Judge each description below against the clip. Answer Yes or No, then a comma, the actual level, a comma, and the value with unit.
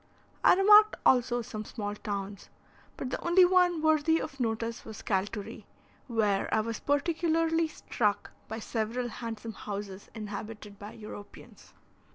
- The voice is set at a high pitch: Yes, high, 230 Hz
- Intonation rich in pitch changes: Yes, wide, 7.0 semitones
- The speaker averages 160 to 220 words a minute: No, slow, 135 wpm